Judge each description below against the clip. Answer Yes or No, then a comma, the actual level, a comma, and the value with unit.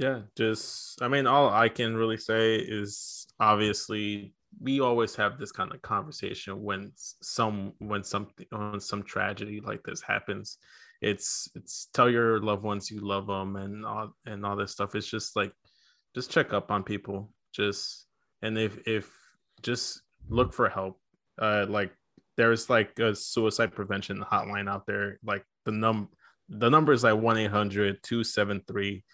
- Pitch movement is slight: Yes, narrow, 1.7 semitones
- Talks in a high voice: No, low, 105 Hz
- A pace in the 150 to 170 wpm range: Yes, average, 160 wpm